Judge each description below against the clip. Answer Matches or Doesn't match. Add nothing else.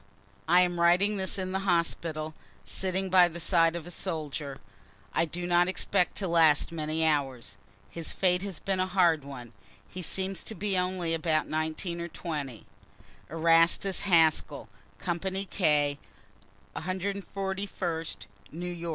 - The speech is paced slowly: Doesn't match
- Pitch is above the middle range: Doesn't match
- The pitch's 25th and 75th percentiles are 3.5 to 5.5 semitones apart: Doesn't match